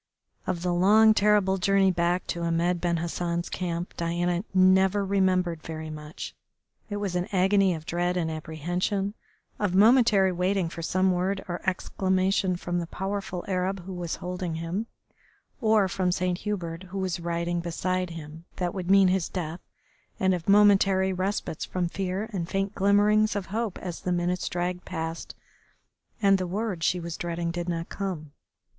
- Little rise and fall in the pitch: Yes, narrow, 2.1 semitones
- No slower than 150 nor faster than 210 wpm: Yes, average, 165 wpm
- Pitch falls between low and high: Yes, medium, 180 Hz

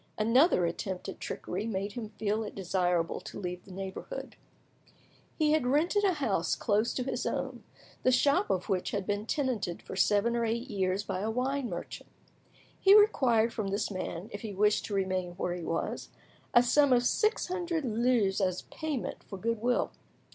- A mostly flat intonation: No, average, 5.1 semitones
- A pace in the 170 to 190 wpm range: Yes, average, 185 wpm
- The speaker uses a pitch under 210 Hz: No, high, 215 Hz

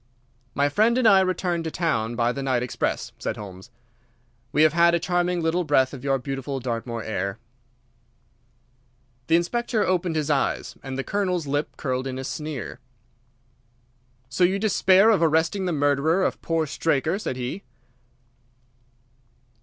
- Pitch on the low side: No, medium, 155 Hz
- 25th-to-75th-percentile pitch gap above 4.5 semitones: Yes, average, 5.2 semitones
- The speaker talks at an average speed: Yes, average, 155 wpm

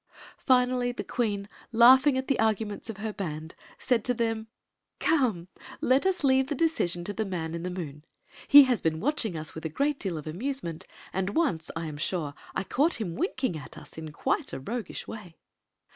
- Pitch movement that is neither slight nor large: No, wide, 7.5 semitones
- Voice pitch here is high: Yes, high, 215 Hz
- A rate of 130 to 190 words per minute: No, average, 200 wpm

